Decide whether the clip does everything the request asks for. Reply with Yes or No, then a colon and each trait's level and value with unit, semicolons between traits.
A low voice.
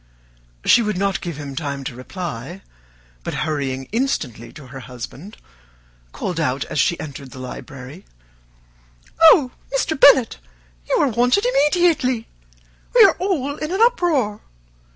No: high, 190 Hz